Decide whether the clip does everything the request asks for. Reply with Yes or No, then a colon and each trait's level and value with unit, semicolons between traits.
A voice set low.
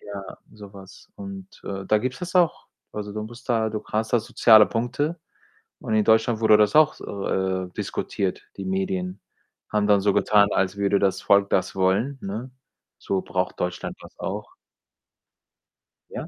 Yes: low, 105 Hz